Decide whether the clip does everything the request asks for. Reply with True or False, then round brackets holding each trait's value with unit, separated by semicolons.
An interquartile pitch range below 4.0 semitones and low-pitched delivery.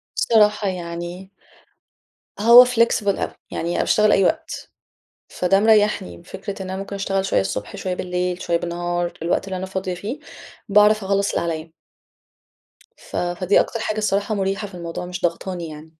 False (2.7 semitones; 190 Hz)